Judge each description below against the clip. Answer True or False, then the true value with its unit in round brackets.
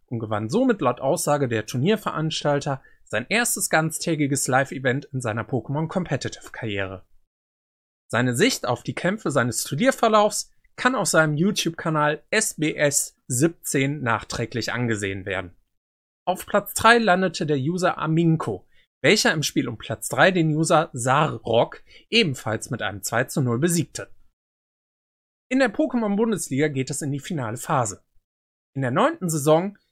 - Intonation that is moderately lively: False (6.5 semitones)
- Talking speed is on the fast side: False (135 wpm)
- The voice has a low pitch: False (150 Hz)